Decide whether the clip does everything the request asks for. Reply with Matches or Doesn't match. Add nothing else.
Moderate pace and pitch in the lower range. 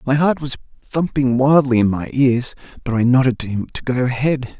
Doesn't match